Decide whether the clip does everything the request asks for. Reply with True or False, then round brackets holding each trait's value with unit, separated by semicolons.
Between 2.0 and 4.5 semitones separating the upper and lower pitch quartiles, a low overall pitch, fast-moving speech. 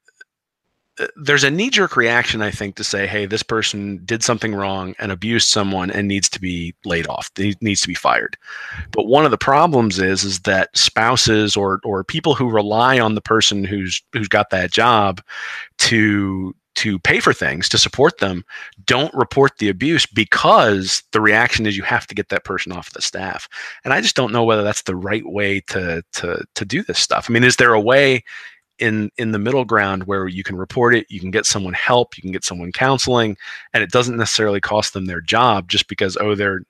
True (3.5 semitones; 105 Hz; 210 wpm)